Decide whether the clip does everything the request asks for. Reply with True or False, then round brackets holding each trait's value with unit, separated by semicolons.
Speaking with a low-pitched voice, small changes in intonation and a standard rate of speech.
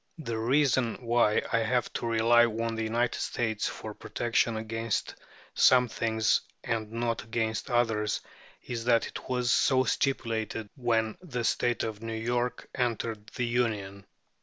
True (115 Hz; 1.5 semitones; 145 wpm)